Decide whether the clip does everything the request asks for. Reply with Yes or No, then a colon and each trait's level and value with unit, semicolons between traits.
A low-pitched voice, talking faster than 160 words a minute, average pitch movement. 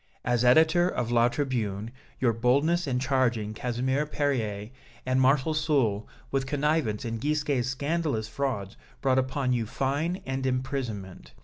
No: low, 130 Hz; slow, 135 wpm; average, 3.6 semitones